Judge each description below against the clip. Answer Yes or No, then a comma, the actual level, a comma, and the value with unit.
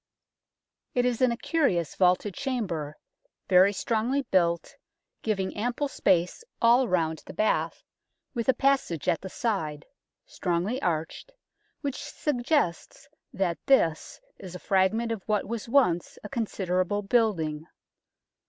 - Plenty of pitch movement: Yes, wide, 5.8 semitones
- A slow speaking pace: Yes, slow, 125 wpm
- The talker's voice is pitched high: Yes, high, 205 Hz